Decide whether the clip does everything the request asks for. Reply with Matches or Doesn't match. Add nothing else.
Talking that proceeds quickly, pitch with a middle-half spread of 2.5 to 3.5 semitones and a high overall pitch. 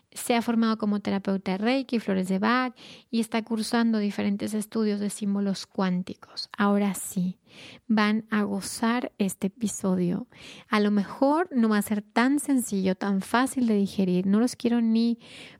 Doesn't match